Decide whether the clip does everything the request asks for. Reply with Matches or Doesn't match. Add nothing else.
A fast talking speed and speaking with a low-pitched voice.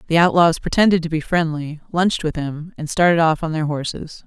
Doesn't match